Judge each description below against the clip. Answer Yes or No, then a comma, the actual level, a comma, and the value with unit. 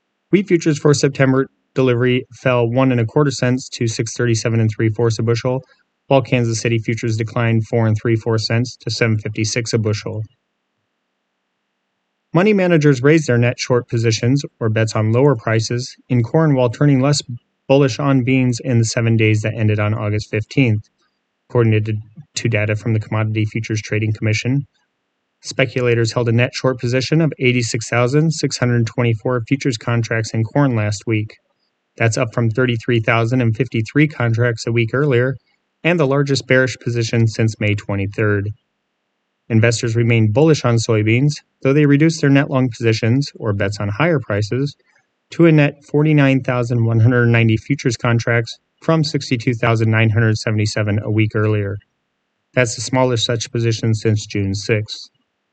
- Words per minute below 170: Yes, average, 150 wpm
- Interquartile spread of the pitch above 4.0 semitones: No, average, 3.0 semitones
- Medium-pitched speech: No, low, 120 Hz